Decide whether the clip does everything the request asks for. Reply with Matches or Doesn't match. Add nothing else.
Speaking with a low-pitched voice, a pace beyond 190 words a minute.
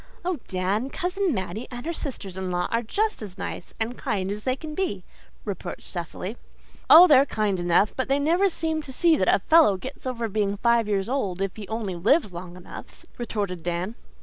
Doesn't match